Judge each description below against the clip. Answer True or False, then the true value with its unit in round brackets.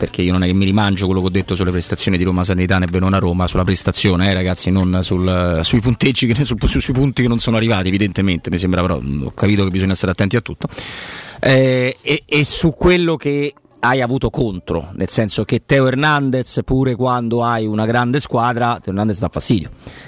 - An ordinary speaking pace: False (205 wpm)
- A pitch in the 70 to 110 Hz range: True (105 Hz)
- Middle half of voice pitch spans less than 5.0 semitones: False (5.4 semitones)